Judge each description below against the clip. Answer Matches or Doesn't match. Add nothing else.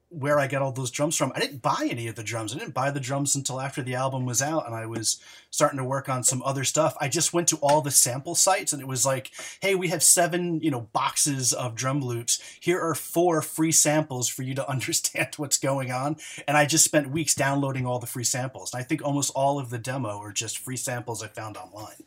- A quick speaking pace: Matches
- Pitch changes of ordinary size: Matches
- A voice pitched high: Doesn't match